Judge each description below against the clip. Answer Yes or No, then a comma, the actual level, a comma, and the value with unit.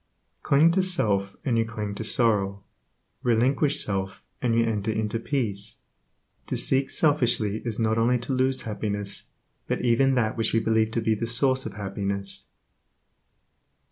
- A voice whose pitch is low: Yes, low, 115 Hz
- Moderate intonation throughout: Yes, average, 3.4 semitones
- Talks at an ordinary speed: Yes, average, 155 wpm